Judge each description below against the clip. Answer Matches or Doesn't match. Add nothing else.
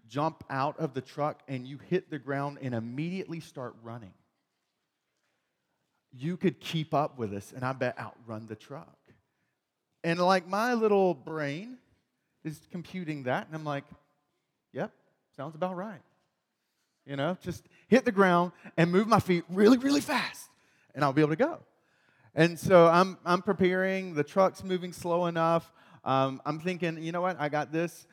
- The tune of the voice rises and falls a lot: Doesn't match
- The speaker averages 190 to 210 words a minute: Doesn't match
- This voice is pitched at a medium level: Matches